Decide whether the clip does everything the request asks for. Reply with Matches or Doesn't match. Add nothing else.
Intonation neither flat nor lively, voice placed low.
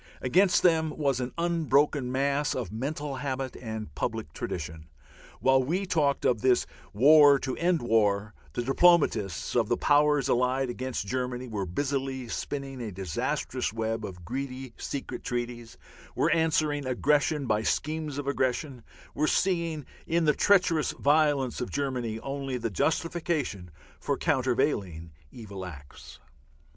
Matches